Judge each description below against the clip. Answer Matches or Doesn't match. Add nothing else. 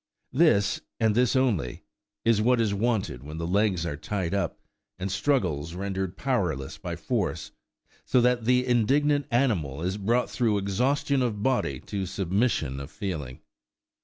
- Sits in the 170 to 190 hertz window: Doesn't match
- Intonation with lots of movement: Matches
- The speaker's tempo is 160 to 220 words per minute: Doesn't match